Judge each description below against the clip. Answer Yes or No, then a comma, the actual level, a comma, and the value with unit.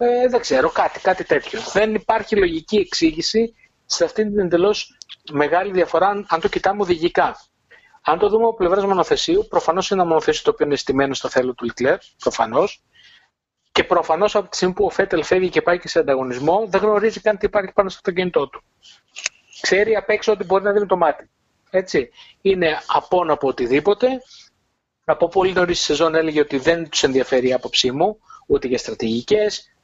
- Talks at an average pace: No, fast, 185 wpm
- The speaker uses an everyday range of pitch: Yes, average, 4.7 semitones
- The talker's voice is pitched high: Yes, high, 195 Hz